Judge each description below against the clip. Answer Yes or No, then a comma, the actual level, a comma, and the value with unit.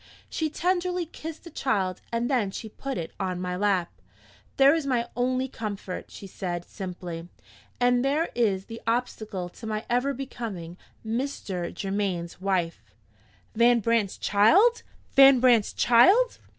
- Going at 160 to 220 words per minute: No, average, 140 wpm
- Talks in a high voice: Yes, high, 230 Hz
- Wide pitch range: Yes, wide, 6.0 semitones